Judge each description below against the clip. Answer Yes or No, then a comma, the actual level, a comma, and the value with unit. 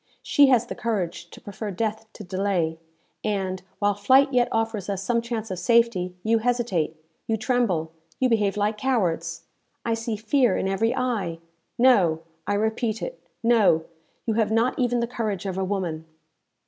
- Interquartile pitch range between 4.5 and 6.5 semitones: No, average, 3.8 semitones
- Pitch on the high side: Yes, high, 215 Hz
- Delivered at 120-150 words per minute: No, average, 170 wpm